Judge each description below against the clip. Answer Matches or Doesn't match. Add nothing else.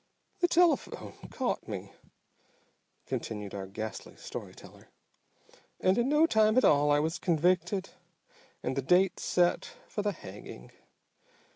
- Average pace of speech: Doesn't match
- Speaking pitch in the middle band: Matches